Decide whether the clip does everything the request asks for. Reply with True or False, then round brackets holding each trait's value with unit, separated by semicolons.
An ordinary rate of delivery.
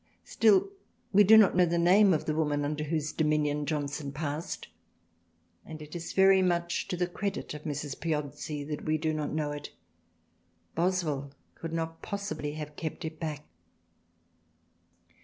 True (160 wpm)